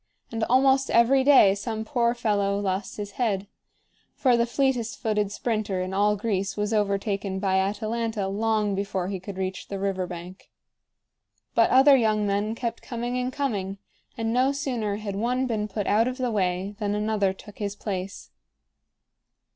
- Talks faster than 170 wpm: No, average, 165 wpm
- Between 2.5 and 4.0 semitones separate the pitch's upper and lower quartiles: Yes, average, 3.0 semitones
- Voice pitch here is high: Yes, high, 210 Hz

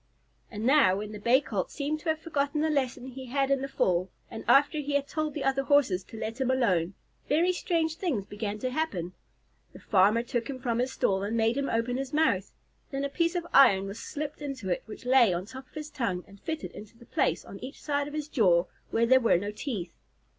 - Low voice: No, very high, 255 Hz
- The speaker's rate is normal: No, fast, 235 wpm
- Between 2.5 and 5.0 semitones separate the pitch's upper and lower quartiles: No, wide, 5.5 semitones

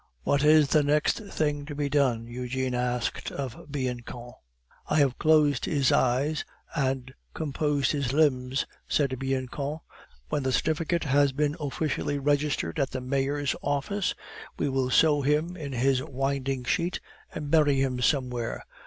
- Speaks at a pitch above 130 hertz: Yes, medium, 140 Hz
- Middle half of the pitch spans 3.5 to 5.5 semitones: No, narrow, 2.4 semitones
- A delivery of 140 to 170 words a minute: Yes, average, 145 wpm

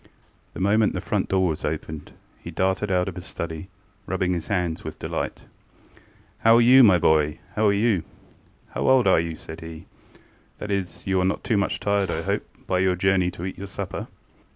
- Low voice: Yes, very low, 95 Hz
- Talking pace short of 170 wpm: No, average, 195 wpm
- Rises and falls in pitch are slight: No, average, 3.1 semitones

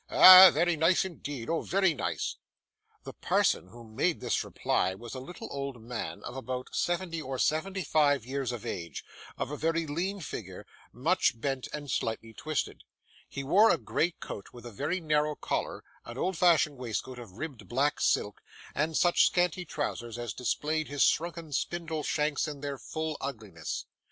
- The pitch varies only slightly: No, average, 5.2 semitones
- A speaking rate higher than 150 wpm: Yes, average, 170 wpm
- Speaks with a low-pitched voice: No, medium, 145 Hz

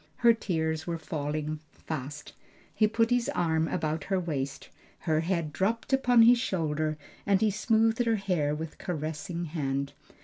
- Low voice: No, medium, 165 Hz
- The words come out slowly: No, average, 150 wpm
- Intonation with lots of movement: Yes, wide, 5.9 semitones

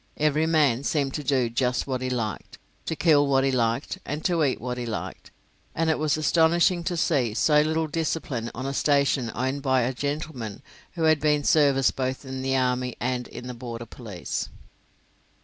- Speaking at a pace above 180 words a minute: Yes, average, 190 wpm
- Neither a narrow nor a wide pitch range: Yes, average, 3.5 semitones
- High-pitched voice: No, low, 135 Hz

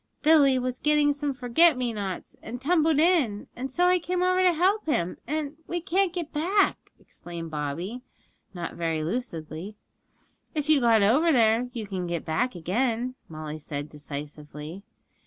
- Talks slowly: No, average, 160 wpm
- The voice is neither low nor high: No, high, 245 Hz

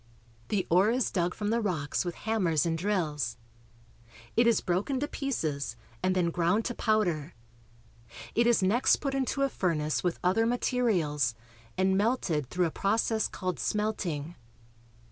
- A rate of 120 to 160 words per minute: Yes, average, 150 wpm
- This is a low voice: No, medium, 185 Hz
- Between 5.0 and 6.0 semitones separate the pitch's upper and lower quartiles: Yes, average, 5.3 semitones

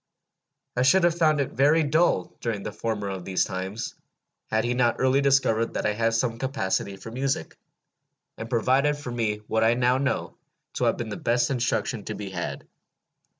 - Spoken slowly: No, average, 190 wpm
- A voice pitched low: Yes, low, 120 Hz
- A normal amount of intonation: Yes, average, 3.9 semitones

